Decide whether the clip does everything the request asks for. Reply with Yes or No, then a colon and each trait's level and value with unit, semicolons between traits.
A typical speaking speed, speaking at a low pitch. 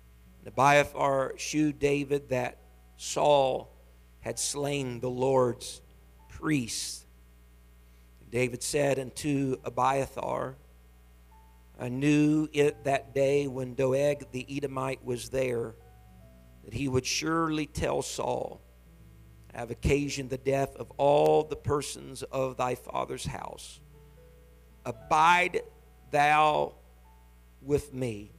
No: slow, 105 wpm; low, 125 Hz